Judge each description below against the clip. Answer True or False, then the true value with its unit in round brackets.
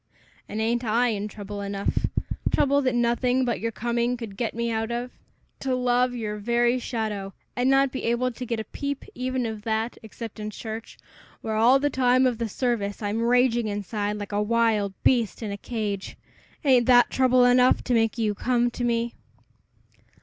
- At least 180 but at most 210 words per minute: True (185 wpm)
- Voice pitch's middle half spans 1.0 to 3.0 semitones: True (2.5 semitones)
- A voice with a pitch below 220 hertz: False (235 Hz)